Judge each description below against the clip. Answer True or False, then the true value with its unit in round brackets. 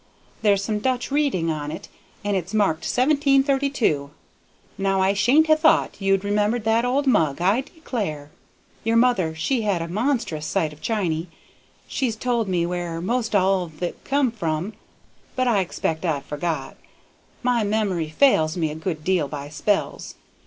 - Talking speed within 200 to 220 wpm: False (160 wpm)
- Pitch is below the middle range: False (195 Hz)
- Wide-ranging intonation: True (6.8 semitones)